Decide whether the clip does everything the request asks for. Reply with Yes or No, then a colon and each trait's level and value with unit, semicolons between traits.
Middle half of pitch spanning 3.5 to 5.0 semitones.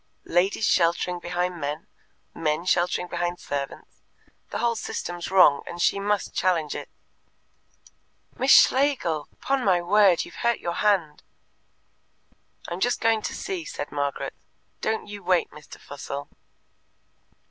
Yes: average, 4.0 semitones